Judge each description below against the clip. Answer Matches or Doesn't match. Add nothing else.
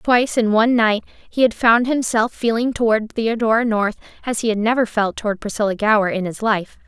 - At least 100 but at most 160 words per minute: Doesn't match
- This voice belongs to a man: Doesn't match